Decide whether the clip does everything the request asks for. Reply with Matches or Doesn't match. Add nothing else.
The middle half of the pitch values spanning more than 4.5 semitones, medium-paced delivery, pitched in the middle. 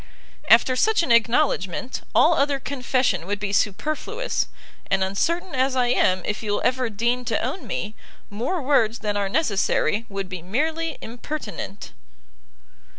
Doesn't match